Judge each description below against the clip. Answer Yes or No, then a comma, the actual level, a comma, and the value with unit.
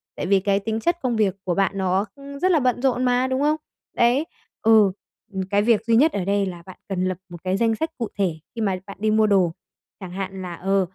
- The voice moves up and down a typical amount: Yes, average, 4.4 semitones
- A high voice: Yes, high, 205 Hz